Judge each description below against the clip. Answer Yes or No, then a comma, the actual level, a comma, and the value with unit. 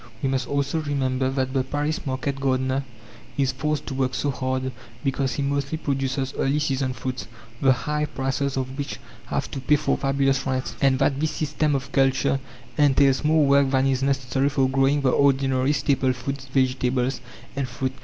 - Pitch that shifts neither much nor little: No, narrow, 1.3 semitones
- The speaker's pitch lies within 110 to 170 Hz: Yes, low, 135 Hz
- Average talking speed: Yes, average, 180 wpm